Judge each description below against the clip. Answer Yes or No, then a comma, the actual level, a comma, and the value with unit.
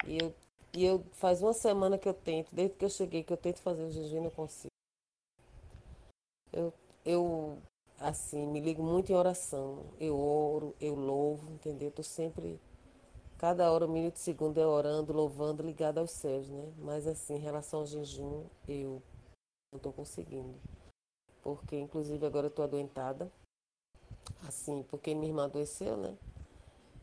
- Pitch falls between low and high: Yes, medium, 155 Hz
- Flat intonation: Yes, narrow, 2.2 semitones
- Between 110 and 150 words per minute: No, average, 165 wpm